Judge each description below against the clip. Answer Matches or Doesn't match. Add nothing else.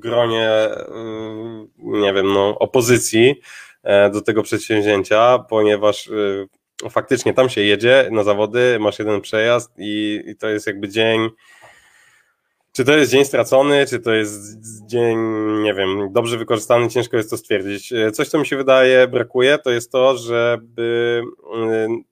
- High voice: Doesn't match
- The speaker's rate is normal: Matches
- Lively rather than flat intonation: Doesn't match